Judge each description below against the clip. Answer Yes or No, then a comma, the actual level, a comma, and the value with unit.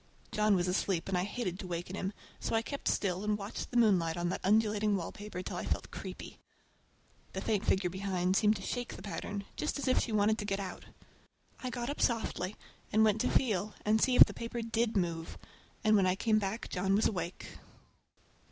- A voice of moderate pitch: No, high, 205 Hz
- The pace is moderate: No, fast, 210 wpm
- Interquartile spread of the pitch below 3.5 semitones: Yes, average, 3.0 semitones